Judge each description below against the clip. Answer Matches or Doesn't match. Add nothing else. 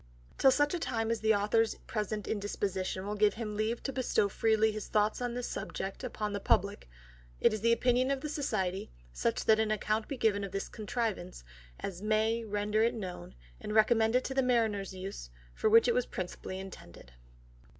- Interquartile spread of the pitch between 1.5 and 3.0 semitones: Matches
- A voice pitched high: Matches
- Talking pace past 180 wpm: Matches